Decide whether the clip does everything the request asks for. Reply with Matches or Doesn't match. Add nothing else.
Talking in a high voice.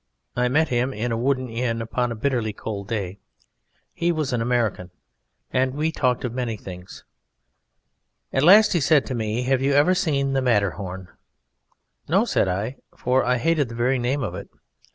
Doesn't match